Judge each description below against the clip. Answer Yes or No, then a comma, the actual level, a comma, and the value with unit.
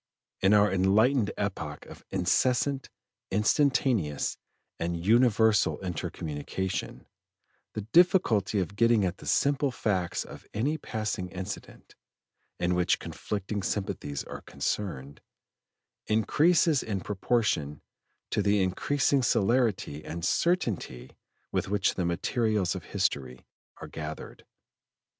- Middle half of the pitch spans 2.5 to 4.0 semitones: No, average, 4.8 semitones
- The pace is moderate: No, slow, 110 wpm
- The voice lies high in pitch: No, low, 100 Hz